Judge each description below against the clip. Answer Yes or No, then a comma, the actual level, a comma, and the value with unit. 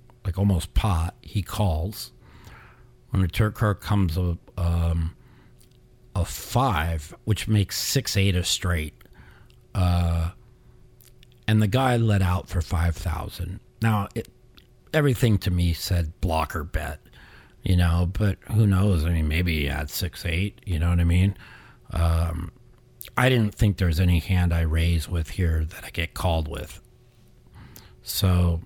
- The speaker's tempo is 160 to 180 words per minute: No, average, 145 wpm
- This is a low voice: Yes, very low, 95 Hz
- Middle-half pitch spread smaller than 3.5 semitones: No, average, 5.0 semitones